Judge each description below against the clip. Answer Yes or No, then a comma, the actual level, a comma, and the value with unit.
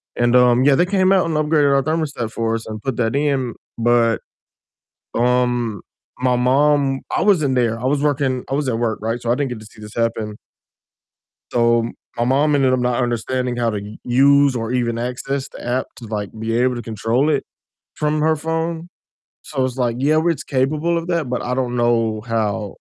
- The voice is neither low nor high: No, low, 125 Hz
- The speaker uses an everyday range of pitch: Yes, average, 3.5 semitones